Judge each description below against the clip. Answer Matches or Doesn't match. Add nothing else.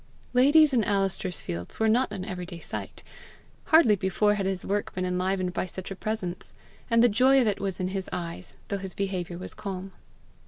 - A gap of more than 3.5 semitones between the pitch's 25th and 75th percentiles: Doesn't match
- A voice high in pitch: Matches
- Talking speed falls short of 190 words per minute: Doesn't match